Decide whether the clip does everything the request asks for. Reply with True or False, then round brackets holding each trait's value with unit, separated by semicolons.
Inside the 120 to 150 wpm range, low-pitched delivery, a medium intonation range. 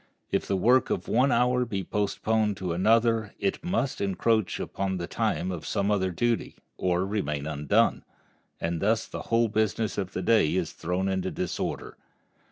False (170 wpm; 100 Hz; 3.8 semitones)